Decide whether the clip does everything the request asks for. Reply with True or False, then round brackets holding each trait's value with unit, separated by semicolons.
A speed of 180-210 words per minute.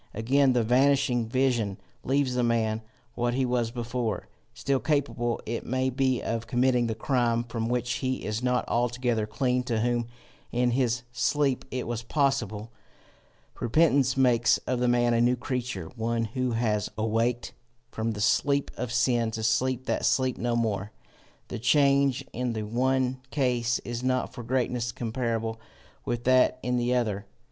False (160 wpm)